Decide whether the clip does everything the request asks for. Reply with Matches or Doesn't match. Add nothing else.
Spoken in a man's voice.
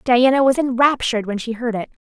Doesn't match